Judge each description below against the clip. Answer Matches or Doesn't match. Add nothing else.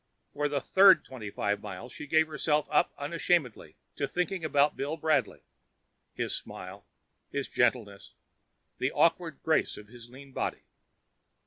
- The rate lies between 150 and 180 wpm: Doesn't match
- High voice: Doesn't match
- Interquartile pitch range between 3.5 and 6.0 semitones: Matches